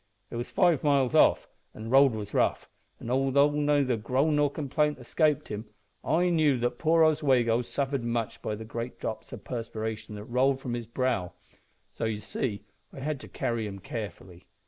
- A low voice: Yes, low, 125 Hz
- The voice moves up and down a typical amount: Yes, average, 4.4 semitones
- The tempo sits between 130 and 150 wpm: No, average, 185 wpm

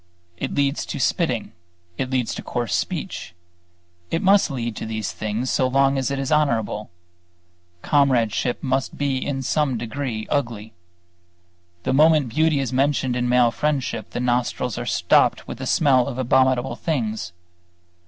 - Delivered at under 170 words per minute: Yes, average, 155 wpm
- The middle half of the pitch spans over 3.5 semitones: No, average, 3.0 semitones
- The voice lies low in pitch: Yes, low, 130 Hz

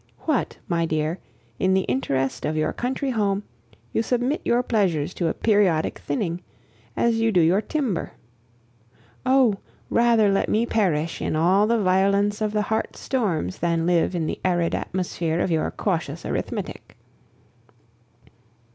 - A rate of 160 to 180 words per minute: No, average, 145 wpm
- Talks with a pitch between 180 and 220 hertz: Yes, high, 190 Hz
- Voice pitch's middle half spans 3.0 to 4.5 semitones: No, average, 5.1 semitones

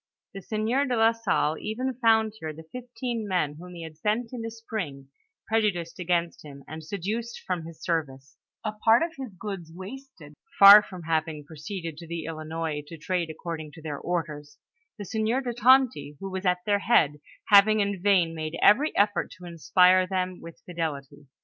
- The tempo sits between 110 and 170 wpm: No, average, 180 wpm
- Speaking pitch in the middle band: Yes, medium, 180 Hz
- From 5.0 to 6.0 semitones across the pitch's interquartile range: Yes, average, 5.3 semitones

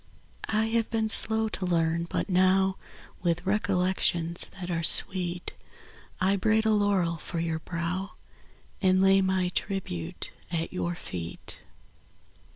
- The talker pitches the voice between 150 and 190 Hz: Yes, medium, 185 Hz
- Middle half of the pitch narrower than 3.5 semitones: Yes, narrow, 2.6 semitones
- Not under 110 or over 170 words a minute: Yes, slow, 135 wpm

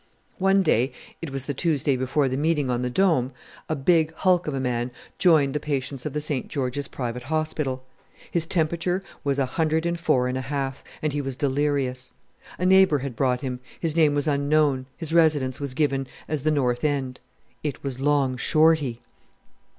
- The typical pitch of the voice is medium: Yes, medium, 145 Hz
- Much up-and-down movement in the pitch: No, average, 3.2 semitones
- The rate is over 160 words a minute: Yes, average, 170 wpm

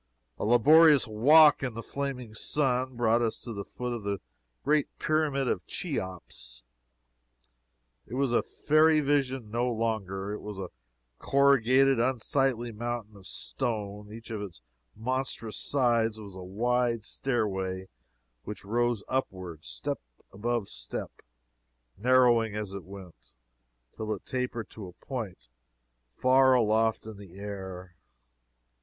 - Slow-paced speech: Yes, slow, 130 wpm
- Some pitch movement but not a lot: Yes, average, 4.3 semitones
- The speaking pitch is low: Yes, low, 115 Hz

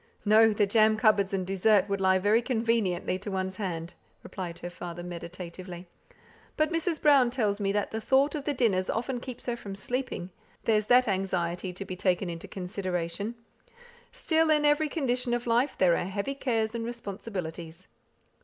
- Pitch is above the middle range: Yes, high, 205 Hz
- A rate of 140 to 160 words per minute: No, average, 170 wpm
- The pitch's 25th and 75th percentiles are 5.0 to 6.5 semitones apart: No, average, 4.6 semitones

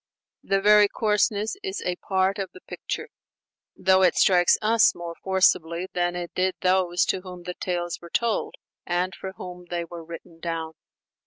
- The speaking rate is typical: Yes, average, 170 wpm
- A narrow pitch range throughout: Yes, narrow, 1.9 semitones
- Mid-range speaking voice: Yes, medium, 180 Hz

